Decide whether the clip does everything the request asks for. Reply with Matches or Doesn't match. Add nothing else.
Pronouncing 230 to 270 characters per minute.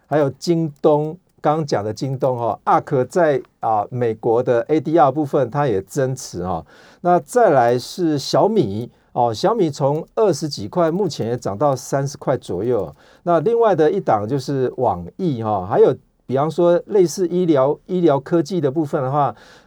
Matches